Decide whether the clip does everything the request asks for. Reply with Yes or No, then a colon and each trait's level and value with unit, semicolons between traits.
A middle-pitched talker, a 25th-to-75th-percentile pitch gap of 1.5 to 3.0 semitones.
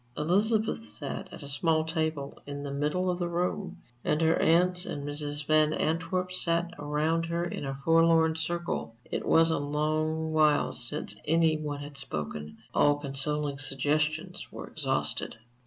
Yes: medium, 155 Hz; narrow, 2.4 semitones